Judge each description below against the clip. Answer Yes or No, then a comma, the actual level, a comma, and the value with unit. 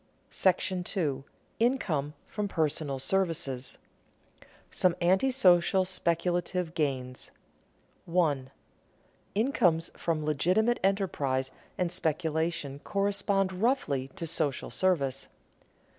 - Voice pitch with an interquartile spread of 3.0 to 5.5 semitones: Yes, average, 4.7 semitones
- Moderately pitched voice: Yes, medium, 170 Hz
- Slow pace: Yes, slow, 90 wpm